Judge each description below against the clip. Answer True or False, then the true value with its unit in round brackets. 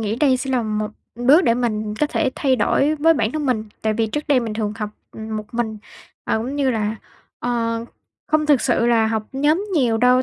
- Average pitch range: True (3.9 semitones)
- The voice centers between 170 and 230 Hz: False (240 Hz)